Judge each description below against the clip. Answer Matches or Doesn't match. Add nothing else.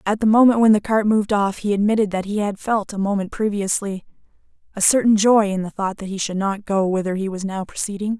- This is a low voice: Doesn't match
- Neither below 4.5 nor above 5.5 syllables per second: Doesn't match